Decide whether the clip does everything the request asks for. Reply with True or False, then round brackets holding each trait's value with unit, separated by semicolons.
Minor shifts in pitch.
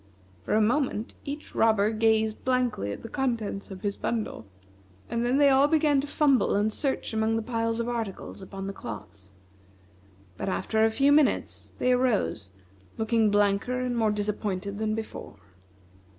False (3.5 semitones)